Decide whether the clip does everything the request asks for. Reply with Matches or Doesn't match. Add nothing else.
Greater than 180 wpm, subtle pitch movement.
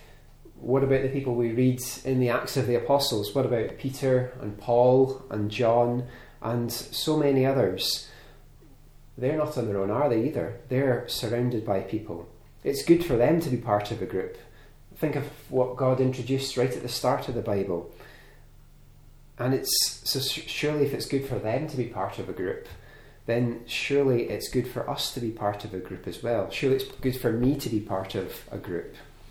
Matches